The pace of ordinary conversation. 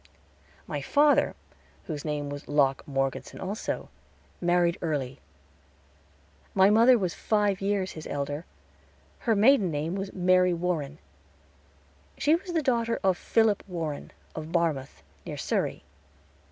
No: slow, 125 wpm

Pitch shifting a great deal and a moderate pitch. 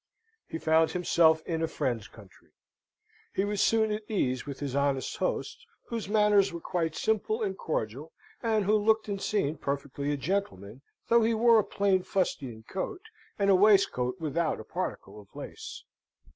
Yes: wide, 6.8 semitones; medium, 180 Hz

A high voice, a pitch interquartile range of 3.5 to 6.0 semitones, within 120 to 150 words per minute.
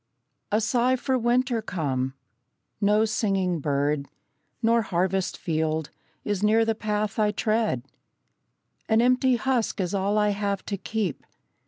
Yes: high, 210 Hz; average, 3.9 semitones; slow, 135 wpm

